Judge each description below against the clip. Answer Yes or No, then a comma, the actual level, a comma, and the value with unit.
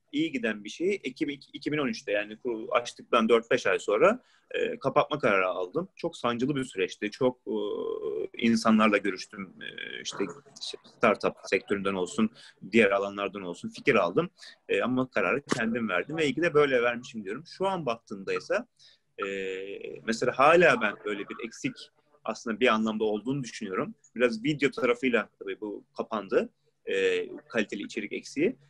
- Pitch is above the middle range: No, low, 130 Hz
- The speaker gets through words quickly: Yes, fast, 150 wpm